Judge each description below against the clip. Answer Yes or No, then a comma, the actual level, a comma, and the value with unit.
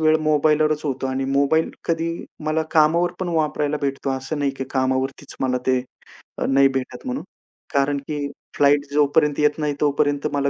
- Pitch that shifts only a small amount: Yes, narrow, 2.1 semitones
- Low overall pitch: No, medium, 145 Hz